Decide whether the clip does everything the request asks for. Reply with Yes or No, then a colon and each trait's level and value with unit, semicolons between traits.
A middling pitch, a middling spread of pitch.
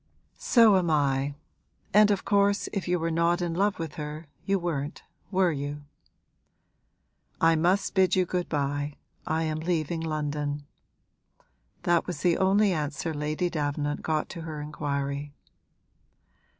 Yes: medium, 160 Hz; average, 3.5 semitones